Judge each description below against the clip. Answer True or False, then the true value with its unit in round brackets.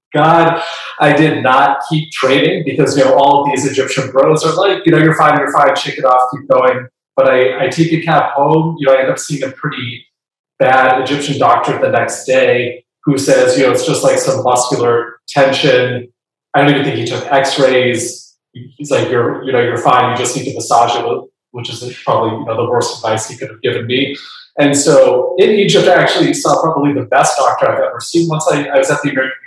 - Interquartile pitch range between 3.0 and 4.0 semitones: True (3.5 semitones)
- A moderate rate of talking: False (230 wpm)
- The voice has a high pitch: False (140 Hz)